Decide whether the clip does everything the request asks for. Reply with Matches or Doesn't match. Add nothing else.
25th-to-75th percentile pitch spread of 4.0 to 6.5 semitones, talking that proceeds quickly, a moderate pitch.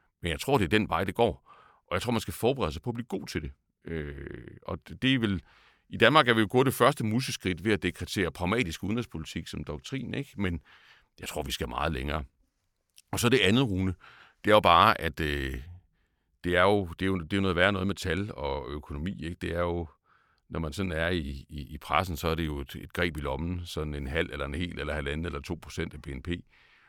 Doesn't match